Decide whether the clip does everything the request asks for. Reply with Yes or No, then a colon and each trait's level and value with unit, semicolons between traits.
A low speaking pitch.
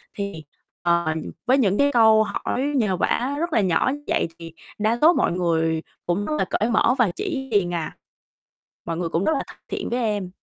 No: high, 210 Hz